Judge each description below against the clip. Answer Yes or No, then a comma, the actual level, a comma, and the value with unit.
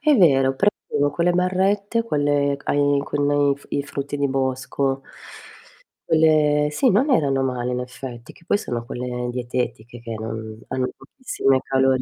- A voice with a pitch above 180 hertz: No, medium, 140 Hz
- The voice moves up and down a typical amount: Yes, average, 3.2 semitones